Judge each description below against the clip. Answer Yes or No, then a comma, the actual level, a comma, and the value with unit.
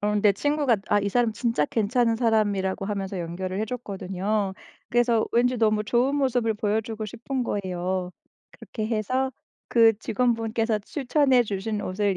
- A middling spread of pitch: Yes, average, 3.1 semitones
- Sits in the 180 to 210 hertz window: No, high, 220 Hz